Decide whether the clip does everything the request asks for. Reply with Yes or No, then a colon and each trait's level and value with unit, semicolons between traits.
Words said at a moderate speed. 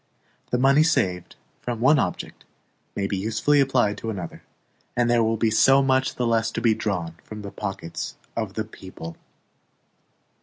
Yes: average, 165 wpm